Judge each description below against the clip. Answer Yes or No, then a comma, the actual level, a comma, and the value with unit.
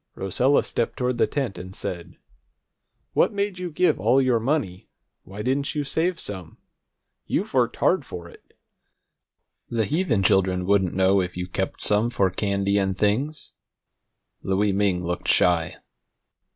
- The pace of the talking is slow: No, average, 150 wpm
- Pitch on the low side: Yes, low, 100 Hz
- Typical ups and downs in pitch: No, wide, 6.0 semitones